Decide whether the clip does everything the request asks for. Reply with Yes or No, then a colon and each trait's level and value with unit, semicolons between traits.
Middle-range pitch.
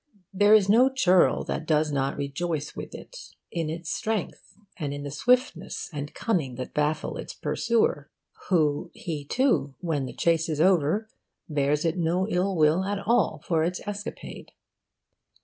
Yes: medium, 165 Hz